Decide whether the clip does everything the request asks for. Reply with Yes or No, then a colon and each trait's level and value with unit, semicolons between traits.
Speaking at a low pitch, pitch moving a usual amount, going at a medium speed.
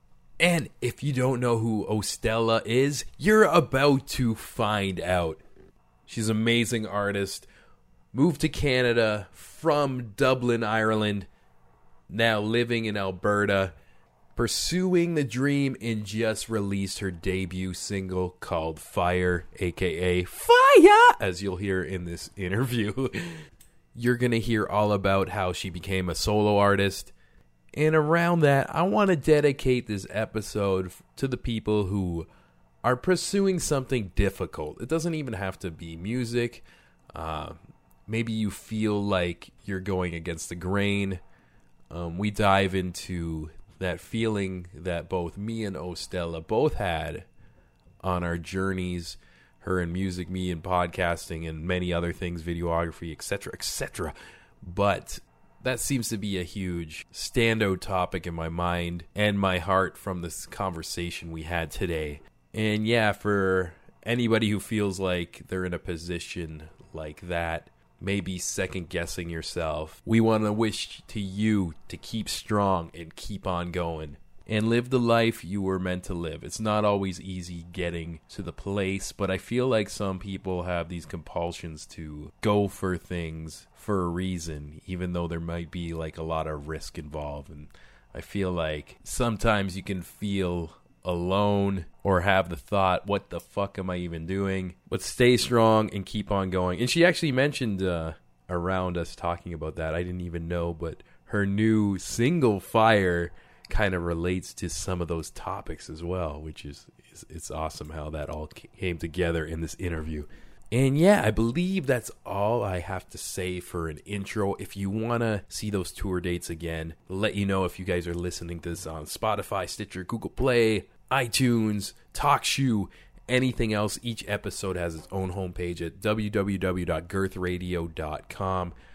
Yes: very low, 95 Hz; average, 4.1 semitones; average, 155 wpm